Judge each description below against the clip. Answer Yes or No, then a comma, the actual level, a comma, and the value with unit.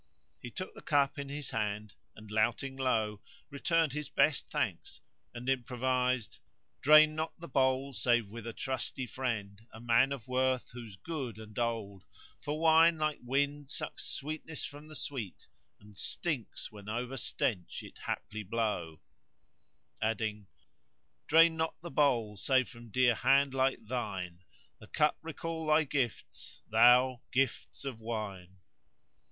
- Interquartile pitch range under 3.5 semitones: No, average, 4.6 semitones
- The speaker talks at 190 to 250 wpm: No, average, 155 wpm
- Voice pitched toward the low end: Yes, low, 125 Hz